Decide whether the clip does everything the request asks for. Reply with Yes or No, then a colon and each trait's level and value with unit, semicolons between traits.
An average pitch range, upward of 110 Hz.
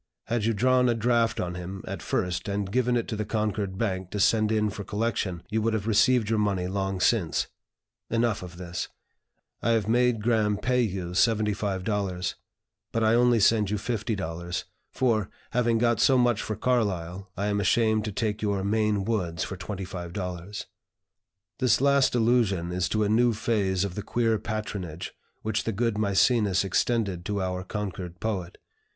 No: average, 3.3 semitones; low, 105 Hz